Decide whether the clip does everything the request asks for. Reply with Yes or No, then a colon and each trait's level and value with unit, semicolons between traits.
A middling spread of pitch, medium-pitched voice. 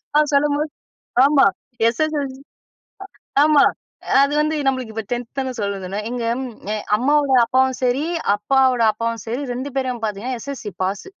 No: average, 3.5 semitones; very high, 260 Hz